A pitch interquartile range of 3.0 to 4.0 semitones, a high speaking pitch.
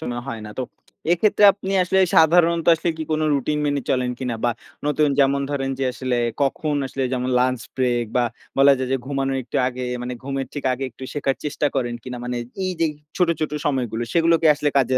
No: average, 3.3 semitones; low, 135 Hz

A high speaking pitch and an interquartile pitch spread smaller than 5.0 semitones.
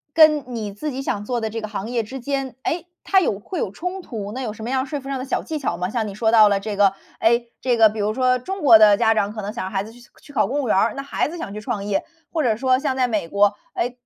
Yes: high, 230 Hz; average, 4.3 semitones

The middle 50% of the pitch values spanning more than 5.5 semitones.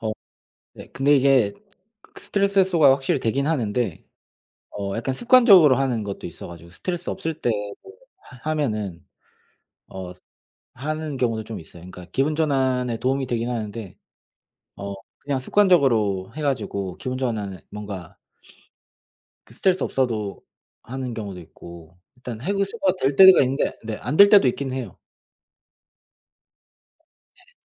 Yes: wide, 6.3 semitones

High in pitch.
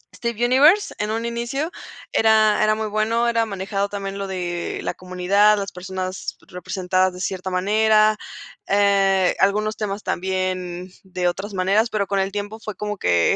Yes: high, 200 Hz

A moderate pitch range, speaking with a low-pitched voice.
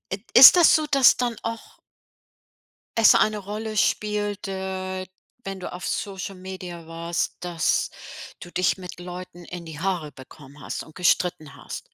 No: average, 3.0 semitones; medium, 185 Hz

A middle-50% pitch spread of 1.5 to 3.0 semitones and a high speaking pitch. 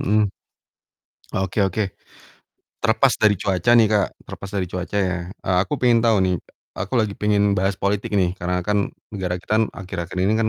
No: narrow, 2.4 semitones; low, 100 Hz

